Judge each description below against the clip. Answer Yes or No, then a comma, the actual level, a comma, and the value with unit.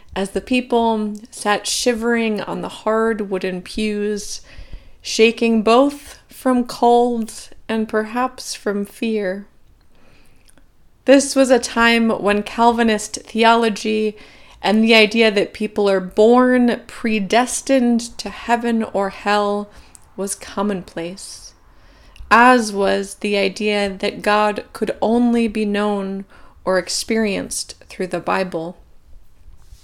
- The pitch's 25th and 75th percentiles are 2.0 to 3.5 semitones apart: Yes, average, 2.8 semitones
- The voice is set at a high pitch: Yes, high, 215 Hz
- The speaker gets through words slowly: Yes, slow, 110 wpm